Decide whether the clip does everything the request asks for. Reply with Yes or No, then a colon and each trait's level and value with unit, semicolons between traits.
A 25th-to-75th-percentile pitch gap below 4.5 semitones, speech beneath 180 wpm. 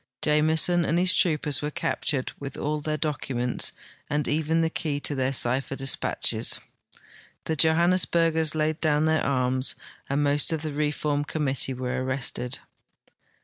Yes: narrow, 2.6 semitones; average, 155 wpm